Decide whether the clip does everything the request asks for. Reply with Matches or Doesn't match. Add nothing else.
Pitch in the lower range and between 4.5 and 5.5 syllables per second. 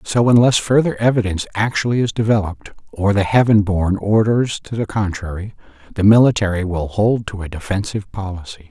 Doesn't match